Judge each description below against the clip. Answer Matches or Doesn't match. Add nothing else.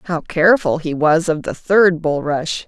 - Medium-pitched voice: Matches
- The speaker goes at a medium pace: Matches